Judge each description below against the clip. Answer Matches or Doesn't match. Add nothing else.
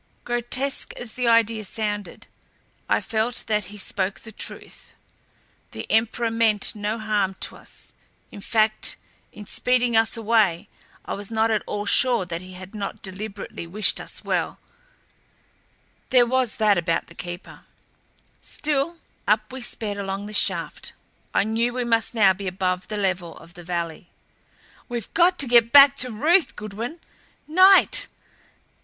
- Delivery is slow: Doesn't match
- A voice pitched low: Doesn't match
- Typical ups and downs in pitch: Matches